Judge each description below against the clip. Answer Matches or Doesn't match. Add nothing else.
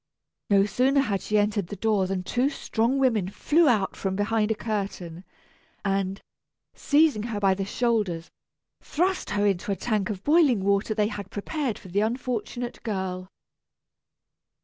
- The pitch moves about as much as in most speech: Matches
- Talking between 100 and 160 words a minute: Matches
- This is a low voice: Doesn't match